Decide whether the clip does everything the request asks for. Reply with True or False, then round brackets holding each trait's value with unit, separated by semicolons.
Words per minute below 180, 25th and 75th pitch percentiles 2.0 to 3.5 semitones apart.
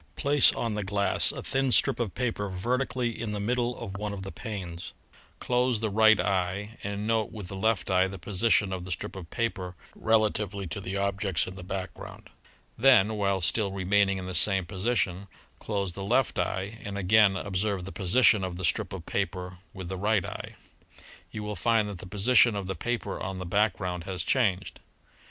False (195 wpm; 2.8 semitones)